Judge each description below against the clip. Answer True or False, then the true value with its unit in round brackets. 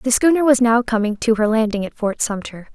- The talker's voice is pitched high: True (230 Hz)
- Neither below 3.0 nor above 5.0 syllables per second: False (5.6 syllables/s)